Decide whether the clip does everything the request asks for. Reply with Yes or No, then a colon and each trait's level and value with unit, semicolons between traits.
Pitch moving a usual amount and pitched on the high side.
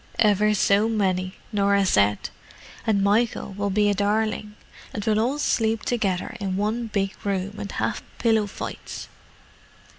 No: narrow, 1.7 semitones; high, 205 Hz